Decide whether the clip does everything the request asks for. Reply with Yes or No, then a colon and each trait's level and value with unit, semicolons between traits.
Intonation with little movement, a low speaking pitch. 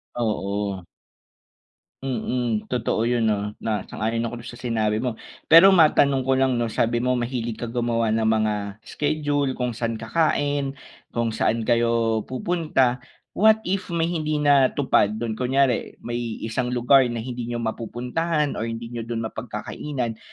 No: average, 3.2 semitones; low, 120 Hz